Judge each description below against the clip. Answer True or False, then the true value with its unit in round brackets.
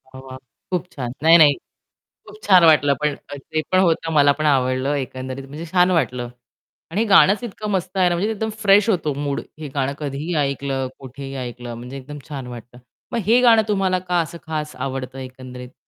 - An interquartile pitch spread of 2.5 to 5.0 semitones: False (5.4 semitones)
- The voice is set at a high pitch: False (145 Hz)